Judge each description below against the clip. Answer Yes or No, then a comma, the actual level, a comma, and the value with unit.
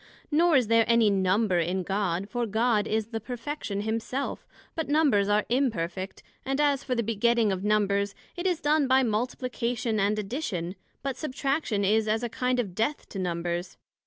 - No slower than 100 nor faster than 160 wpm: No, average, 175 wpm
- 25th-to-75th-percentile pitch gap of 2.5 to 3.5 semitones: No, average, 4.3 semitones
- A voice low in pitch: No, high, 225 Hz